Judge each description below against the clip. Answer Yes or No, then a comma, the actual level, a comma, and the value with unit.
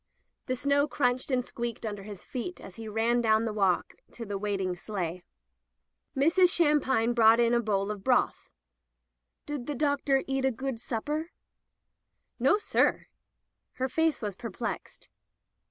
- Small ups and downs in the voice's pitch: No, average, 4.4 semitones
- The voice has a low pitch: No, high, 240 Hz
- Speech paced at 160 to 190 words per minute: No, average, 150 wpm